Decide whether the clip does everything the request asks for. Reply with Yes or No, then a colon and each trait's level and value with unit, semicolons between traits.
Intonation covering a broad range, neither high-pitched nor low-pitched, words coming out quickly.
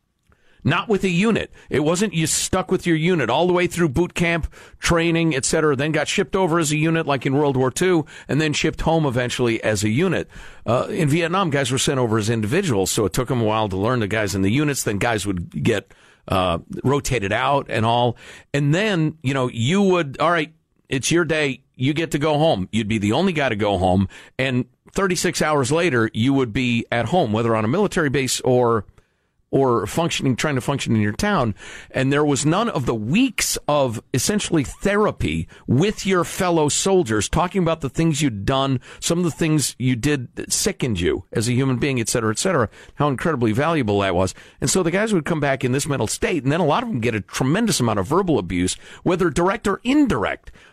Yes: wide, 6.1 semitones; medium, 145 Hz; fast, 225 wpm